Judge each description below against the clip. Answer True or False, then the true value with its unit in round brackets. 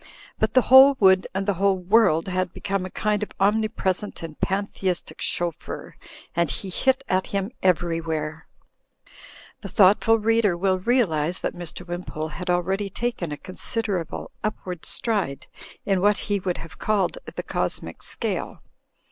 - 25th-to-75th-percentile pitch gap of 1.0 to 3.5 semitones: True (3.1 semitones)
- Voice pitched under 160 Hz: False (190 Hz)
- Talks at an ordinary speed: True (155 wpm)